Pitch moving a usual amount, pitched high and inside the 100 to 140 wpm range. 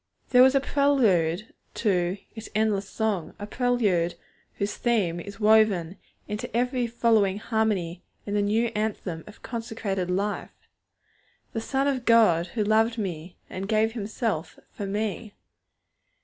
Yes: average, 3.1 semitones; high, 210 Hz; slow, 135 wpm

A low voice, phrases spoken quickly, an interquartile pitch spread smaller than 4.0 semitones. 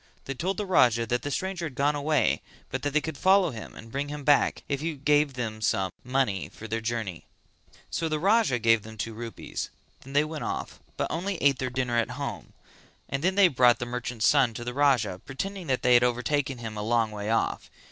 No: low, 130 Hz; fast, 225 wpm; average, 4.3 semitones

